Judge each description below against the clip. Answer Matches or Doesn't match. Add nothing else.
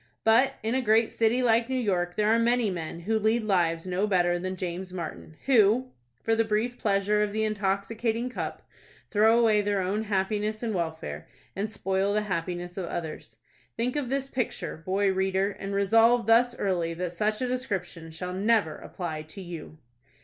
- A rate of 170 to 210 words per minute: Matches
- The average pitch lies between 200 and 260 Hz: Matches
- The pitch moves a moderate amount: Matches